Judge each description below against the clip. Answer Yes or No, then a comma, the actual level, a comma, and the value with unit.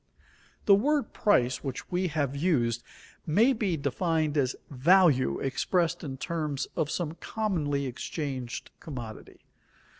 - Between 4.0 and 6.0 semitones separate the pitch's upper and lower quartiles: Yes, average, 5.2 semitones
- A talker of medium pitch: Yes, medium, 150 Hz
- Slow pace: Yes, slow, 125 wpm